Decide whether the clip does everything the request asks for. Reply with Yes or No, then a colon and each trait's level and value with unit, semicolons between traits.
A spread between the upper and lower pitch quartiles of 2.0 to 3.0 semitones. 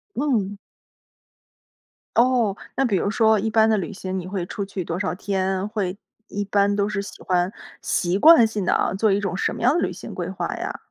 Yes: narrow, 2.5 semitones